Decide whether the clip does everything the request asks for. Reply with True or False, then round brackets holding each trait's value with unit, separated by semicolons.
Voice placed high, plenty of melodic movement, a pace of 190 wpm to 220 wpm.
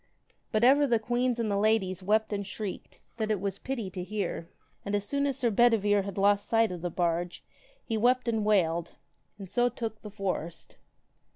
False (210 Hz; 3.4 semitones; 200 wpm)